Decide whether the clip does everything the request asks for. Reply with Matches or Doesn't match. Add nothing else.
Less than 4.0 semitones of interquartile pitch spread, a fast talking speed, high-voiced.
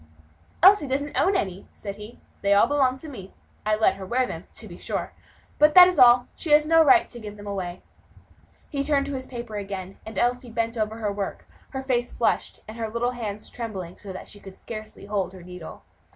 Doesn't match